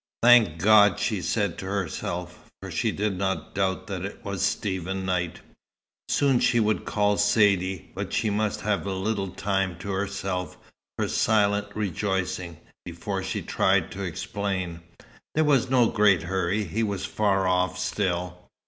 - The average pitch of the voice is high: No, very low, 95 Hz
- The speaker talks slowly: No, average, 155 wpm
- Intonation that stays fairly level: Yes, narrow, 2.2 semitones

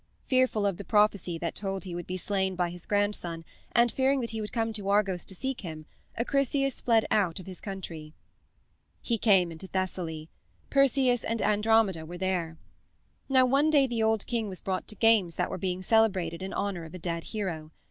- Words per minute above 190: Yes, average, 200 wpm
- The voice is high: Yes, high, 195 Hz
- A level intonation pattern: No, average, 4.2 semitones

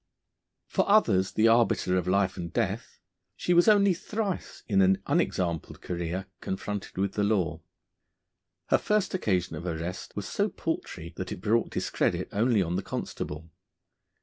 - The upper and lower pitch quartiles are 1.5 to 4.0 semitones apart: No, average, 4.6 semitones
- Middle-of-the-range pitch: No, very low, 95 Hz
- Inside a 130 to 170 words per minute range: Yes, average, 150 wpm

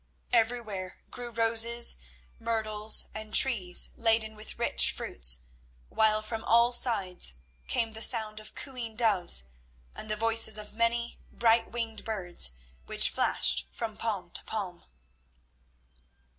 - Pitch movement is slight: Yes, narrow, 1.7 semitones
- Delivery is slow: Yes, slow, 125 wpm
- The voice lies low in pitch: No, high, 220 Hz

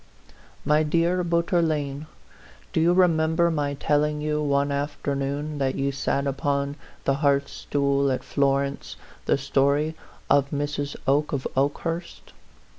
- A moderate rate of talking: No, slow, 125 wpm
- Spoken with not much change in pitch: Yes, narrow, 2.0 semitones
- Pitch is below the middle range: No, medium, 145 Hz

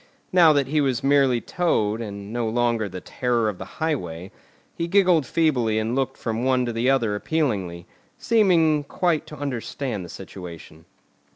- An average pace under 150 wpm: No, average, 165 wpm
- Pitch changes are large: Yes, wide, 6.0 semitones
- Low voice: Yes, low, 125 Hz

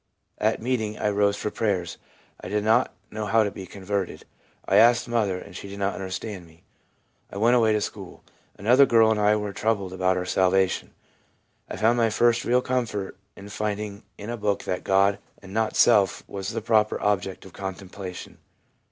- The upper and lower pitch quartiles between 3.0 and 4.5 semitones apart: No, narrow, 2.5 semitones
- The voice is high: No, low, 105 Hz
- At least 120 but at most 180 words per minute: No, average, 190 wpm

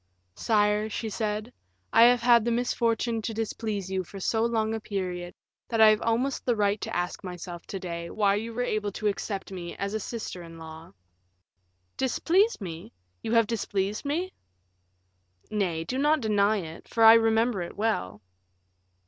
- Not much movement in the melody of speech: No, average, 3.3 semitones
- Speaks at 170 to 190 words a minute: Yes, average, 175 wpm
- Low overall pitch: No, high, 215 Hz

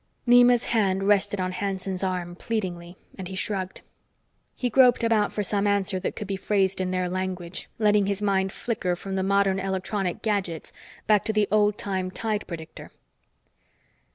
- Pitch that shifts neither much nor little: No, narrow, 2.0 semitones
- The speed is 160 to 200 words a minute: Yes, average, 165 wpm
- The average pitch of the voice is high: Yes, high, 195 Hz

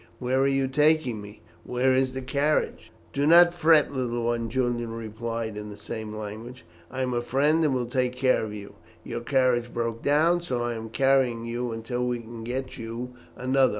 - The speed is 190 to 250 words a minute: Yes, average, 200 wpm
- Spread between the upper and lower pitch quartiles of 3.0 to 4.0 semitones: No, narrow, 2.5 semitones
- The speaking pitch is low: Yes, low, 125 Hz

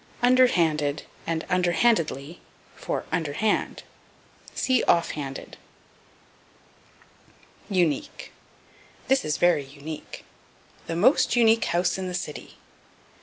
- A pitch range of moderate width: No, wide, 6.3 semitones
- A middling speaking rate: No, slow, 105 wpm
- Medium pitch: Yes, medium, 175 Hz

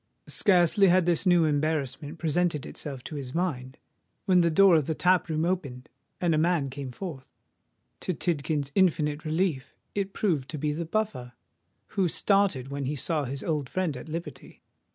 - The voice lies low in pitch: No, medium, 155 Hz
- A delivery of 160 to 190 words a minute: Yes, average, 175 wpm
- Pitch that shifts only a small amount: No, average, 4.0 semitones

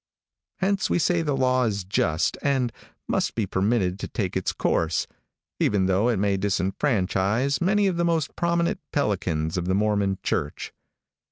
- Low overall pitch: Yes, low, 105 Hz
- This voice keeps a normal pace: Yes, average, 160 wpm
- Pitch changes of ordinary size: No, wide, 7.0 semitones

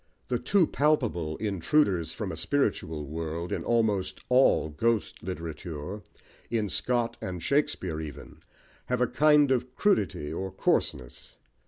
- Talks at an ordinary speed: No, slow, 130 wpm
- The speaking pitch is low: Yes, low, 100 Hz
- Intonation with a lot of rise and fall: Yes, wide, 7.6 semitones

